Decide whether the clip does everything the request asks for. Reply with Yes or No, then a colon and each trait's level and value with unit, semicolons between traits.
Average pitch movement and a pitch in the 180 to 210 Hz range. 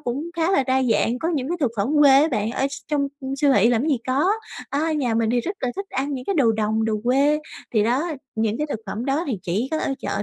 No: average, 4.6 semitones; very high, 265 Hz